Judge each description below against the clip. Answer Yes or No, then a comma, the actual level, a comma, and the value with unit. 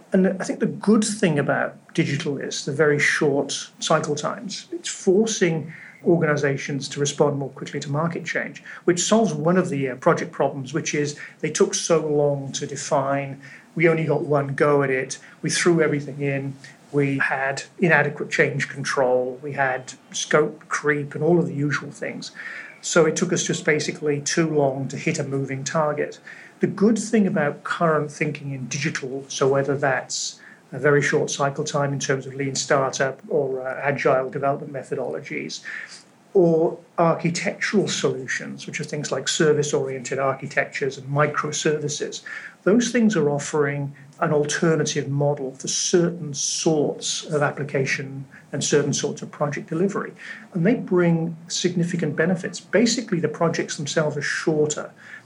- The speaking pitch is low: No, medium, 150 Hz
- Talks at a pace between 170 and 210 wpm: No, average, 155 wpm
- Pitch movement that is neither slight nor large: Yes, average, 3.7 semitones